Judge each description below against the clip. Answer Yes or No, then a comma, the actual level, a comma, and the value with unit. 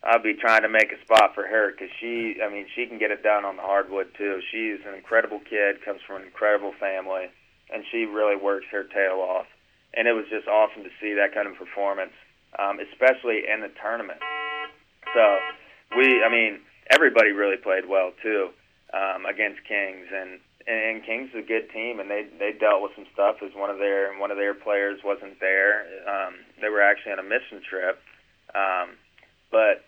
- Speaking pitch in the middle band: No, low, 100 Hz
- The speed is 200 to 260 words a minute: Yes, fast, 205 wpm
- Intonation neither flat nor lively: No, narrow, 2.1 semitones